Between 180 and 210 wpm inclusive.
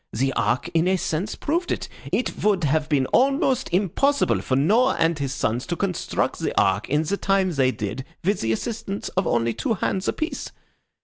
Yes: average, 190 wpm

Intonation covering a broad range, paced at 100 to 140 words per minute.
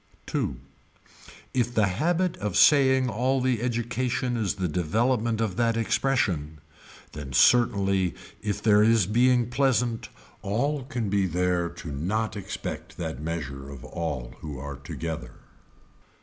Yes: wide, 6.4 semitones; slow, 135 wpm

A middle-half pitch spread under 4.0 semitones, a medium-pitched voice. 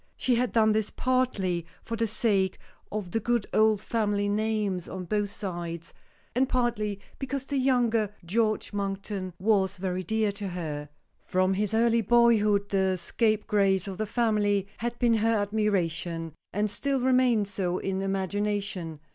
No: average, 3.0 semitones; high, 205 Hz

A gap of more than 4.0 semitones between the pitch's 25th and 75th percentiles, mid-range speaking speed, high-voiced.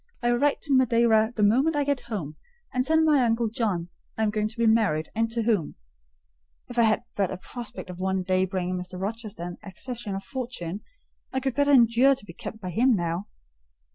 No: average, 4.6 semitones; fast, 215 wpm; high, 220 Hz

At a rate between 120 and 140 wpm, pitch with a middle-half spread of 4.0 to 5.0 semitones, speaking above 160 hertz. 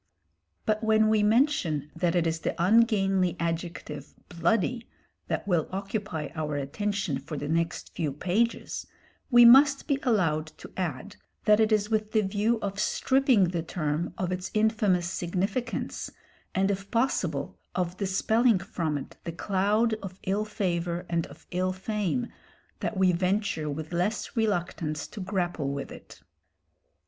No: average, 150 wpm; average, 4.3 semitones; high, 190 Hz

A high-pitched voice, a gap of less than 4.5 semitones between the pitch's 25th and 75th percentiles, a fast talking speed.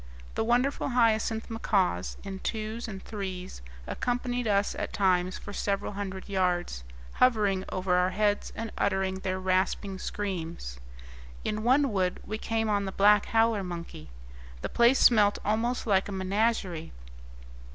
No: high, 200 Hz; average, 3.0 semitones; average, 140 wpm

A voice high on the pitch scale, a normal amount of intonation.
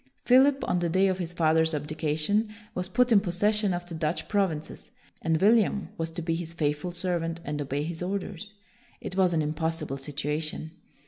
No: medium, 170 Hz; average, 3.5 semitones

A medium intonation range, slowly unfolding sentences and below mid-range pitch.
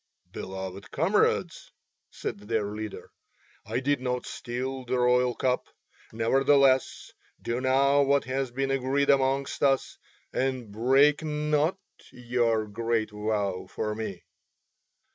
Yes: average, 3.5 semitones; slow, 115 wpm; low, 125 Hz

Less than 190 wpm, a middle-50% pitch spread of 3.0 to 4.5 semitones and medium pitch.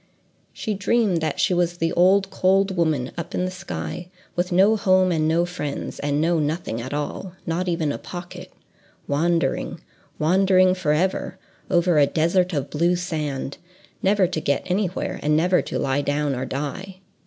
Yes: average, 170 wpm; average, 3.7 semitones; medium, 175 Hz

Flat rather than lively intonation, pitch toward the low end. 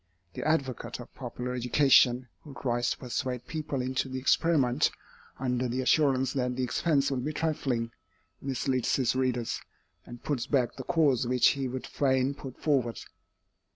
Yes: narrow, 2.0 semitones; low, 130 Hz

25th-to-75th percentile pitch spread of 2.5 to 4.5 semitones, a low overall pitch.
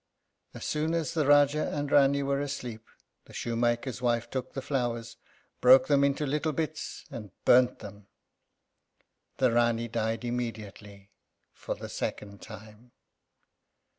Yes: average, 3.7 semitones; low, 125 Hz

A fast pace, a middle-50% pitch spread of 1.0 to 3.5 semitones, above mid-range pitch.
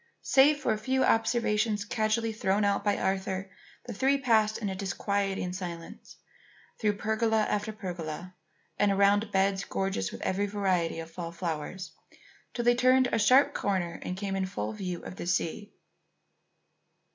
No: average, 155 wpm; average, 2.9 semitones; high, 200 Hz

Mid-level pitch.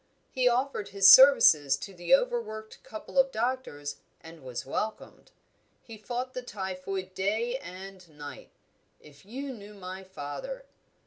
No: high, 200 Hz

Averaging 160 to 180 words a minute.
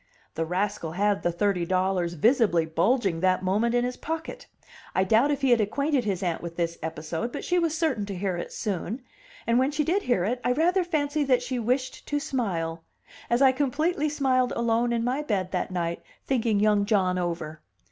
No: average, 200 wpm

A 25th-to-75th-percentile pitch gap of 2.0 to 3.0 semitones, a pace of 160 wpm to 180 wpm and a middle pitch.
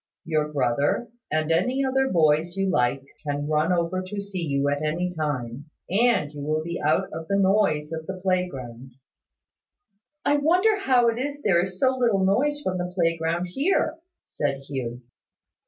No: average, 5.3 semitones; average, 170 wpm; medium, 170 Hz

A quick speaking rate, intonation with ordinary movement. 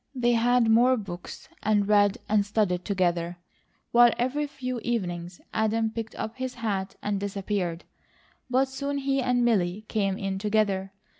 No: average, 150 wpm; average, 3.8 semitones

